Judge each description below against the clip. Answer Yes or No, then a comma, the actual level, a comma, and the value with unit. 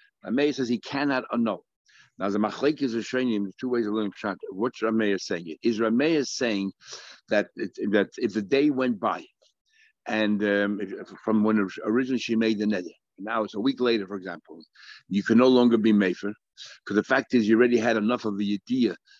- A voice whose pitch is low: Yes, low, 115 Hz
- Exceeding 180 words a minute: Yes, fast, 205 wpm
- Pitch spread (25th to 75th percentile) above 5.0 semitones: No, average, 3.6 semitones